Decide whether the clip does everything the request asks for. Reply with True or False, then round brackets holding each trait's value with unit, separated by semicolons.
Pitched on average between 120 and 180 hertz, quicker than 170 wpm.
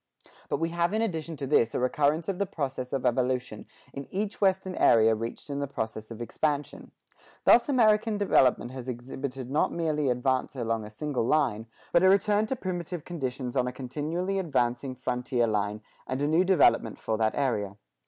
True (135 Hz; 185 wpm)